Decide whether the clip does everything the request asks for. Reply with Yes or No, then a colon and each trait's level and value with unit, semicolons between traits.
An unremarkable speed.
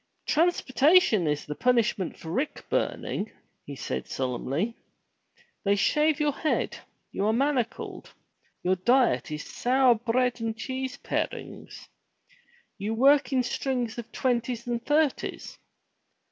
No: slow, 120 wpm